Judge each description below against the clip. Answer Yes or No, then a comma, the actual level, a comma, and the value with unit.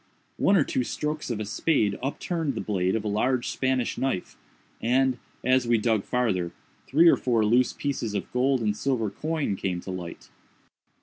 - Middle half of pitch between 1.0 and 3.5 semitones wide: No, average, 4.3 semitones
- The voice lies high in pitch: No, low, 120 Hz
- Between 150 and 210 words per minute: Yes, average, 180 wpm